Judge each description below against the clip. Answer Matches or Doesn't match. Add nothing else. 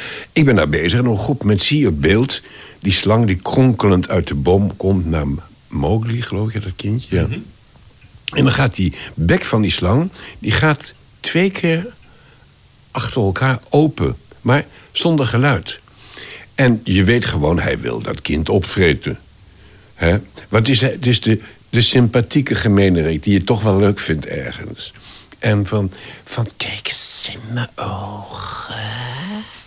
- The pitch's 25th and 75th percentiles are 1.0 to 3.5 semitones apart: Doesn't match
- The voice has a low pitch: Matches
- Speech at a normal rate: Matches